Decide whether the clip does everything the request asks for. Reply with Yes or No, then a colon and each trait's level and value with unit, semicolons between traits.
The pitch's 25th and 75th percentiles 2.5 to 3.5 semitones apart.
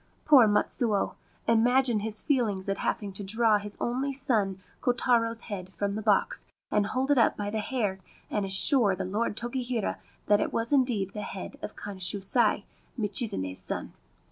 Yes: average, 3.2 semitones